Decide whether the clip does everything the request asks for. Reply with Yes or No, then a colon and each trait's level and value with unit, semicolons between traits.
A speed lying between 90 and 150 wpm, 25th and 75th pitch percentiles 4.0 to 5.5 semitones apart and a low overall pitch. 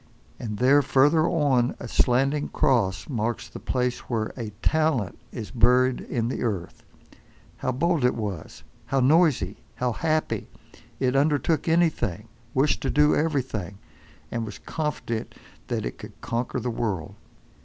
Yes: average, 145 wpm; average, 4.5 semitones; low, 125 Hz